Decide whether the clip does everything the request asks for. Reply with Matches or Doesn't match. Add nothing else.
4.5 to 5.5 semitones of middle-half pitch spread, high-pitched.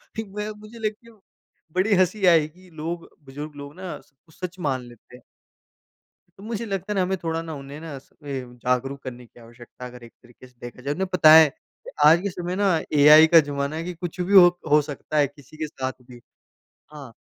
Doesn't match